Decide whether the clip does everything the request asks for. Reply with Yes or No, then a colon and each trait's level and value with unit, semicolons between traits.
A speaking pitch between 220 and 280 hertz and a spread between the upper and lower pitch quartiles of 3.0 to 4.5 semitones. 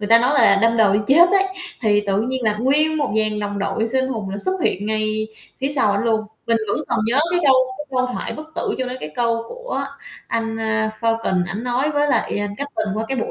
Yes: high, 230 Hz; average, 3.9 semitones